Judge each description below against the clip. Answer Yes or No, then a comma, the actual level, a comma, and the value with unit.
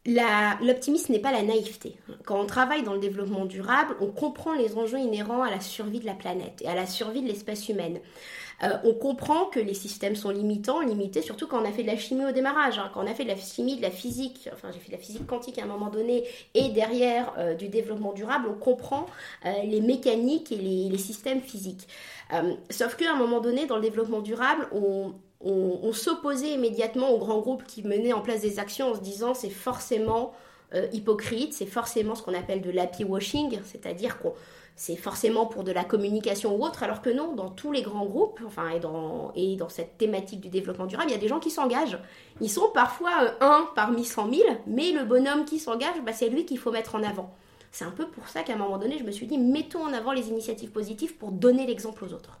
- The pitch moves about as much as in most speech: Yes, average, 4.2 semitones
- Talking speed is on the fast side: Yes, fast, 235 wpm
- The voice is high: Yes, high, 225 Hz